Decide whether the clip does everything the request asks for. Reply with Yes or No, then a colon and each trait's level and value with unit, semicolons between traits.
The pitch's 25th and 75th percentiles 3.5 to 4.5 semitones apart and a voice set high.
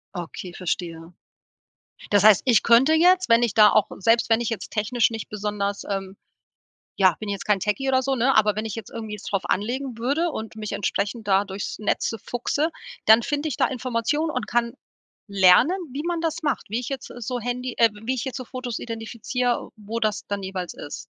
Yes: average, 3.8 semitones; high, 230 Hz